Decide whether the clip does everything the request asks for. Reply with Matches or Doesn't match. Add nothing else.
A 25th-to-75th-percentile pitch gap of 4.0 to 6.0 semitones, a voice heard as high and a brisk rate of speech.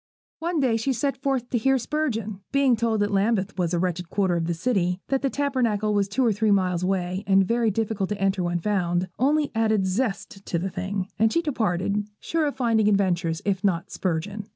Matches